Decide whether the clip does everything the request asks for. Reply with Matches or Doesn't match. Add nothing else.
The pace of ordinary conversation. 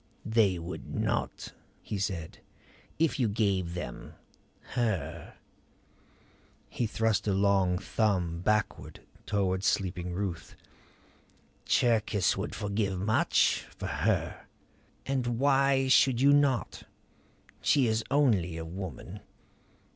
Doesn't match